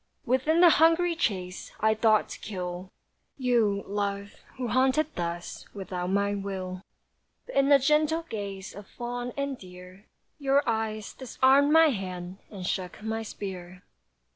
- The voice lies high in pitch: Yes, high, 215 Hz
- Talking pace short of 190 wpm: Yes, average, 140 wpm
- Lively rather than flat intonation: Yes, wide, 6.0 semitones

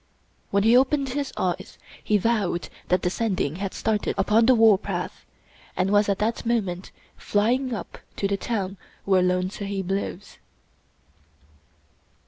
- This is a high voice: Yes, high, 205 Hz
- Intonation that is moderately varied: Yes, average, 3.3 semitones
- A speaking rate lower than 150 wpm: Yes, average, 140 wpm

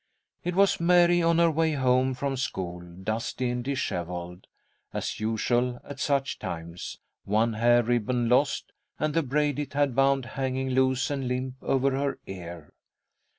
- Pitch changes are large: No, average, 4.0 semitones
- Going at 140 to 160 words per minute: Yes, average, 150 wpm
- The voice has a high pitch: No, low, 130 Hz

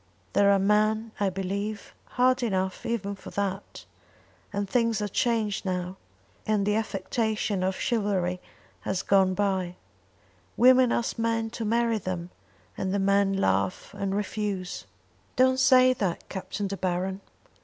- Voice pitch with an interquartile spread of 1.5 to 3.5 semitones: Yes, average, 2.9 semitones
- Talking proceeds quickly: No, average, 140 wpm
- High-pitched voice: Yes, high, 200 Hz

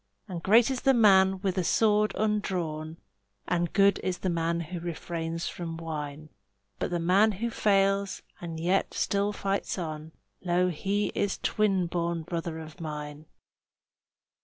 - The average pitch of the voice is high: No, medium, 180 Hz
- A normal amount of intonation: Yes, average, 3.3 semitones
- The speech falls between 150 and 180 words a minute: Yes, average, 155 wpm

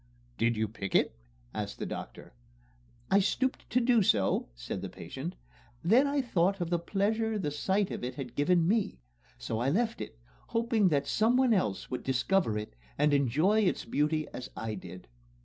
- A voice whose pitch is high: No, medium, 170 Hz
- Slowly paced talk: No, average, 180 wpm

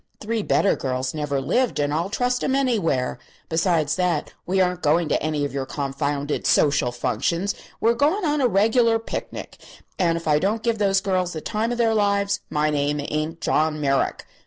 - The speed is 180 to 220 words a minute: Yes, average, 185 wpm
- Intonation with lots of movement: Yes, wide, 6.7 semitones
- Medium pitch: Yes, medium, 170 Hz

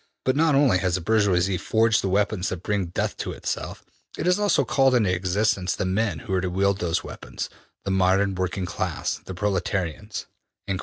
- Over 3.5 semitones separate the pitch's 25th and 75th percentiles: No, average, 3.2 semitones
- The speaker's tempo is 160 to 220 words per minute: Yes, average, 190 wpm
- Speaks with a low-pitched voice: Yes, very low, 95 Hz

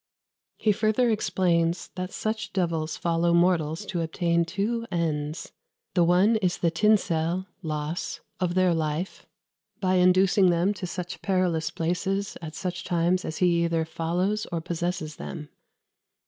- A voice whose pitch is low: No, medium, 175 Hz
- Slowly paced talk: No, average, 145 wpm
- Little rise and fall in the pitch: Yes, narrow, 2.2 semitones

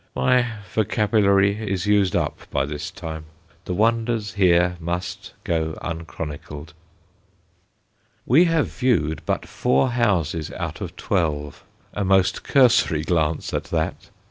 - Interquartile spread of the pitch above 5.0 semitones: Yes, wide, 5.4 semitones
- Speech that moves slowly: Yes, slow, 120 wpm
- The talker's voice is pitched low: Yes, very low, 95 Hz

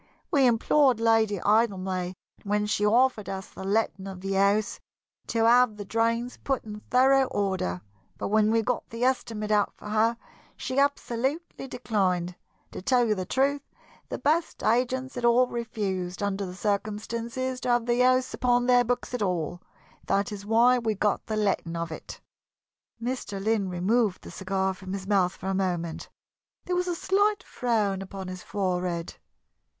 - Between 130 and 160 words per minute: No, average, 170 wpm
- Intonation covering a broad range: No, average, 4.2 semitones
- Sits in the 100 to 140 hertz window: No, high, 215 Hz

